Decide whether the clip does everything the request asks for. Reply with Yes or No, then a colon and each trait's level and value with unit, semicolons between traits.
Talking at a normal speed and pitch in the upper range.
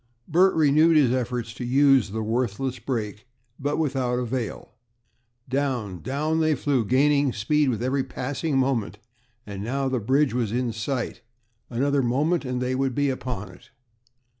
No: average, 155 wpm; low, 130 Hz